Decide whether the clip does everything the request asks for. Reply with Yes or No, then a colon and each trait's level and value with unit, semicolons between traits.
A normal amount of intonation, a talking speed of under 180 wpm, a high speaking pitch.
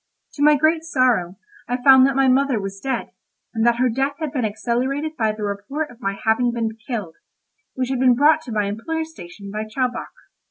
No: average, 4.1 semitones; fast, 205 wpm; very high, 250 Hz